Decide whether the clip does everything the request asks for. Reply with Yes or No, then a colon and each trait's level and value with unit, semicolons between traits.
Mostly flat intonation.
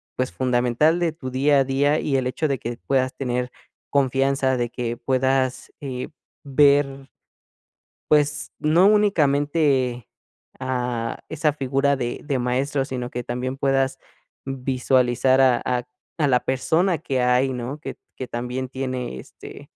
Yes: narrow, 2.2 semitones